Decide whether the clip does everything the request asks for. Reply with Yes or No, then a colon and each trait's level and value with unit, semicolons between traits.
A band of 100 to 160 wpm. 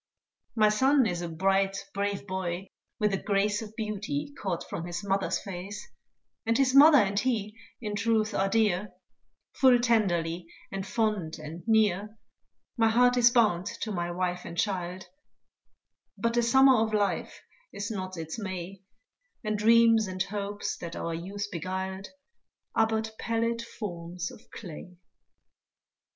Yes: average, 145 wpm